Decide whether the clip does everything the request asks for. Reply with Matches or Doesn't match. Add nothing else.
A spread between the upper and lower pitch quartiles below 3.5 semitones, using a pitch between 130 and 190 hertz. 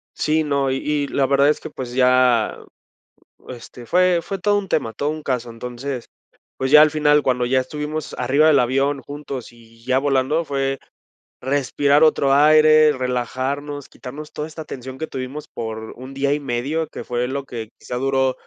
Matches